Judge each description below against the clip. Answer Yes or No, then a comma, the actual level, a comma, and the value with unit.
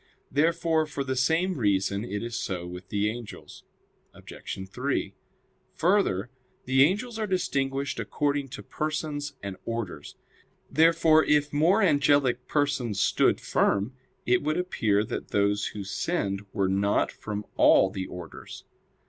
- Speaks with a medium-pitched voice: No, low, 130 Hz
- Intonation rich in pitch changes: Yes, wide, 7.3 semitones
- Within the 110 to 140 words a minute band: Yes, slow, 135 wpm